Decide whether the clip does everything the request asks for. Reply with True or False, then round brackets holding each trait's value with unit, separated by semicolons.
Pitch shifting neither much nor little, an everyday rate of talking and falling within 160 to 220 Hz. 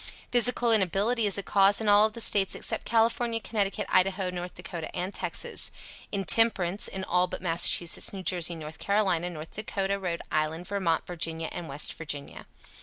True (3.3 semitones; 165 wpm; 190 Hz)